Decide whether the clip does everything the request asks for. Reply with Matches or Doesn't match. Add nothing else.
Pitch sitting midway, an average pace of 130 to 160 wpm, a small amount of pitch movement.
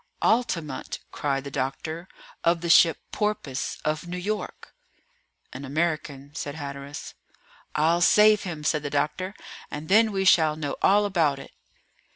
Doesn't match